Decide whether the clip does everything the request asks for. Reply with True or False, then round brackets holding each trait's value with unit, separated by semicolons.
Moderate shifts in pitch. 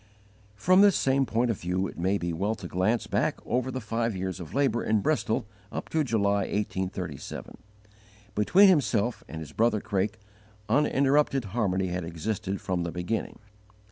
True (4.9 semitones)